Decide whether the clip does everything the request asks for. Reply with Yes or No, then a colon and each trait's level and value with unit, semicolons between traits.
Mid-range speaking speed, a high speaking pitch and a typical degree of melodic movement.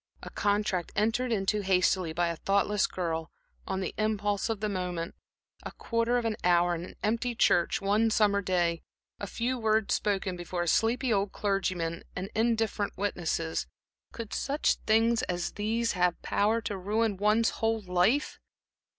Yes: average, 160 wpm; high, 205 Hz; average, 3.7 semitones